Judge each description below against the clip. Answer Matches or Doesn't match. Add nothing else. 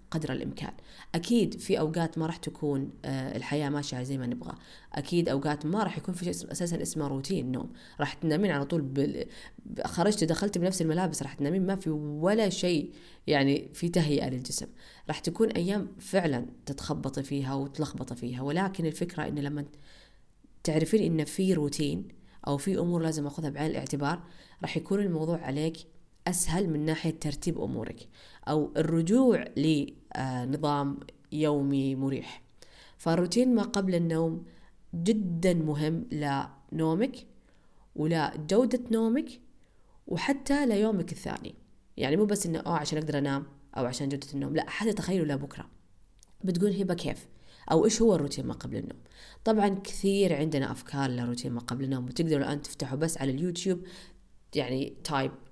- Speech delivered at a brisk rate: Matches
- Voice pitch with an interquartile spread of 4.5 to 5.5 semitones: Matches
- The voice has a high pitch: Doesn't match